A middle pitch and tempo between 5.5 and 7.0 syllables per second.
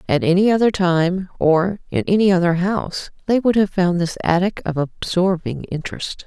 No: medium, 180 Hz; 5.0 syllables/s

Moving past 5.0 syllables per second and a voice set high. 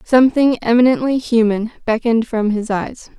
Yes: 5.2 syllables/s; high, 235 Hz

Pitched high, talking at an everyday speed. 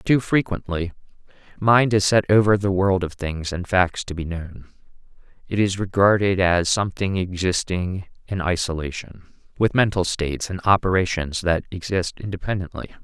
No: very low, 95 Hz; average, 145 wpm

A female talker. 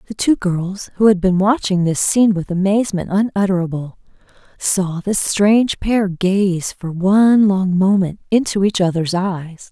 Yes: female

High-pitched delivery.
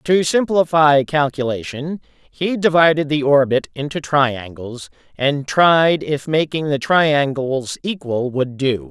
No: medium, 145 Hz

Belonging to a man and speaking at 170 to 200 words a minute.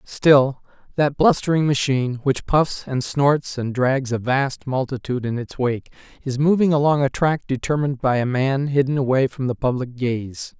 Yes: male; average, 175 wpm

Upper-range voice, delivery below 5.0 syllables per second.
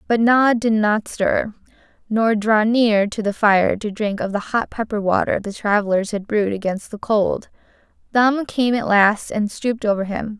Yes: high, 215 Hz; 4.5 syllables/s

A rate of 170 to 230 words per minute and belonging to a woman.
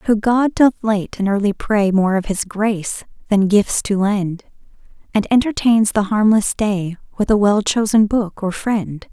Yes: average, 180 wpm; female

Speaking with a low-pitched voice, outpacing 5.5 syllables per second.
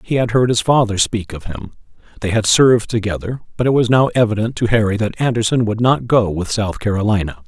Yes: low, 110 Hz; 6.0 syllables/s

